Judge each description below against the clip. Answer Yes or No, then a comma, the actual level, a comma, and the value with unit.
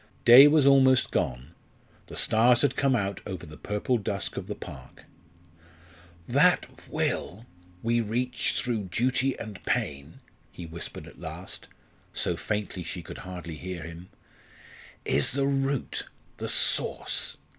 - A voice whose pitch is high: No, low, 105 Hz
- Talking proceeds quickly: No, slow, 135 wpm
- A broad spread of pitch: Yes, wide, 6.7 semitones